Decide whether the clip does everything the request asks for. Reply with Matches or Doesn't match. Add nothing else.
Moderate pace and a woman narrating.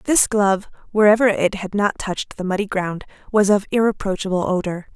Matches